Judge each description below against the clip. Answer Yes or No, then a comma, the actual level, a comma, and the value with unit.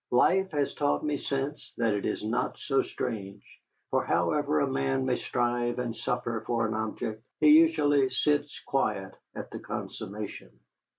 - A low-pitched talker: Yes, low, 120 Hz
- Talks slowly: No, average, 160 wpm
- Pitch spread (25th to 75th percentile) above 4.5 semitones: Yes, average, 5.0 semitones